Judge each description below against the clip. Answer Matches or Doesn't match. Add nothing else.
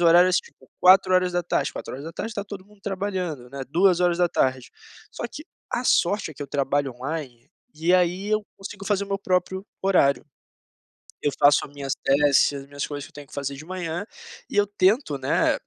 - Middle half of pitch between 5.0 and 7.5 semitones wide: Matches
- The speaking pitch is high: Doesn't match